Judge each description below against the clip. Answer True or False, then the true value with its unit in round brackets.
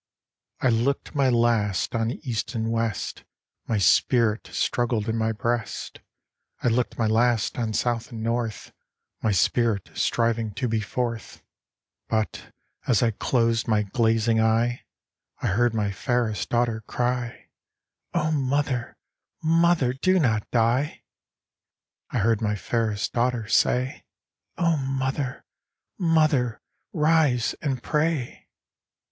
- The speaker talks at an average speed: False (130 wpm)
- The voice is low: True (120 Hz)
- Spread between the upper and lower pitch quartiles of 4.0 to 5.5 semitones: False (2.5 semitones)